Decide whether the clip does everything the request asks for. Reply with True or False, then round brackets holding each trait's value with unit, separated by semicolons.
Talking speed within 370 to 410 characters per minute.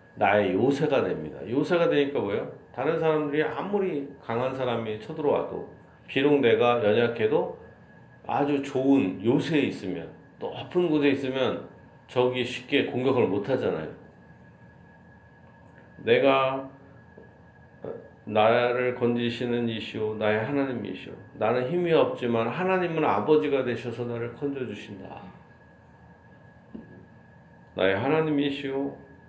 False (255 characters per minute)